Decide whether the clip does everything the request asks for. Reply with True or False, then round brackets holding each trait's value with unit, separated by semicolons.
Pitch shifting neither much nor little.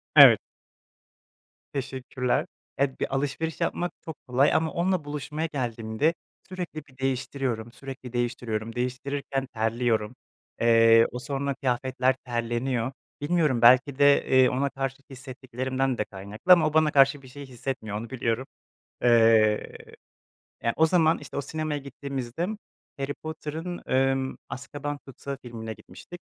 True (3.0 semitones)